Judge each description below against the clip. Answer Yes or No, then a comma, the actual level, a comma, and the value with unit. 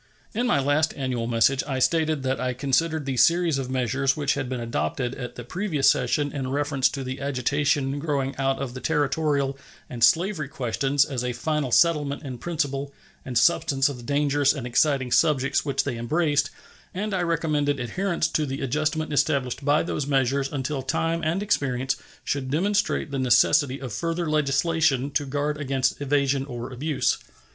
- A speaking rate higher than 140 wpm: Yes, average, 175 wpm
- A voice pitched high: No, medium, 140 Hz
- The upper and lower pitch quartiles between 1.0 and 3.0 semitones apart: Yes, average, 2.7 semitones